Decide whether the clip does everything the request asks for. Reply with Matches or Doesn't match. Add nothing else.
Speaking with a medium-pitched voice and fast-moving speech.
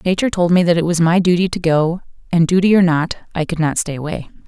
Matches